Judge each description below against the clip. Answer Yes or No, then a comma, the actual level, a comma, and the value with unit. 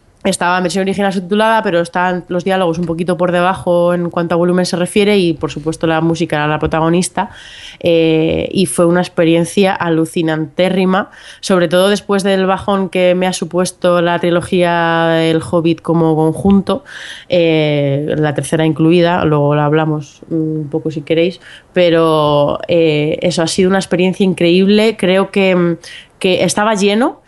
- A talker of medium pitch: Yes, medium, 175 Hz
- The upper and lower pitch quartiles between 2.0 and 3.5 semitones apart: Yes, narrow, 2.4 semitones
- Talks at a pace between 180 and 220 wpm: No, average, 160 wpm